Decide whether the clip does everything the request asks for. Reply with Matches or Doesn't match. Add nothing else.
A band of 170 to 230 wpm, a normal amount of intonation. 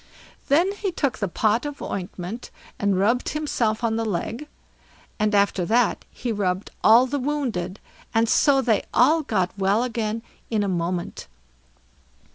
Doesn't match